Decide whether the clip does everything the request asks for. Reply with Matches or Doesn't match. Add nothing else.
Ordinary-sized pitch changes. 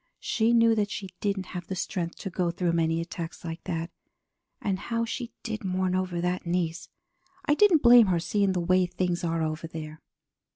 Matches